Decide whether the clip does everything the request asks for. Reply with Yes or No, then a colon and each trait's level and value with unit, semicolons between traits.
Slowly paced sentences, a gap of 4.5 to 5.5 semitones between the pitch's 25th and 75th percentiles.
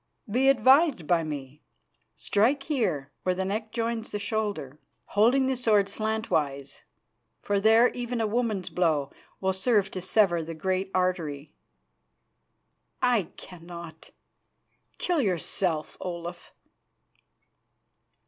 Yes: slow, 110 wpm; average, 5.1 semitones